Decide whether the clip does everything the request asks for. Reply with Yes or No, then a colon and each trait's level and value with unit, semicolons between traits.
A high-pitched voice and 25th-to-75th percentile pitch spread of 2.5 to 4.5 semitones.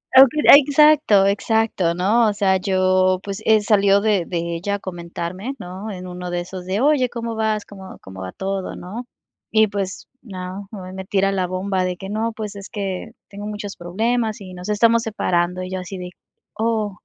Yes: high, 195 Hz; average, 2.9 semitones